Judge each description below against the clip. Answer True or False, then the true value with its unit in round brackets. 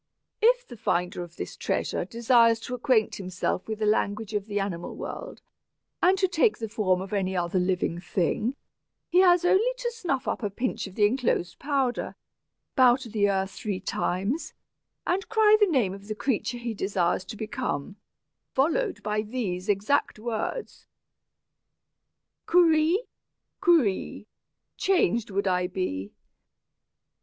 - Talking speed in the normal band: True (150 wpm)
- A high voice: True (220 Hz)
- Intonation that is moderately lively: False (6.7 semitones)